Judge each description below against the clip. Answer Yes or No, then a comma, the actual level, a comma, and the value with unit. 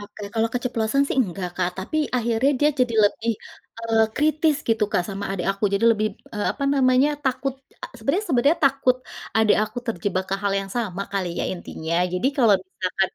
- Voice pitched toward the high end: Yes, high, 225 Hz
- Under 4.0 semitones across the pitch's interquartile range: No, average, 4.6 semitones